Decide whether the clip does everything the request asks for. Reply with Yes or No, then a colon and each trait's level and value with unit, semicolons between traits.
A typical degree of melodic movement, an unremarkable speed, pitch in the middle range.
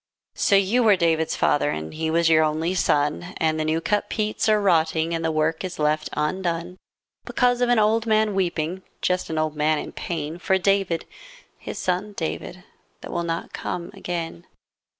Yes: average, 3.5 semitones; average, 185 wpm; medium, 170 Hz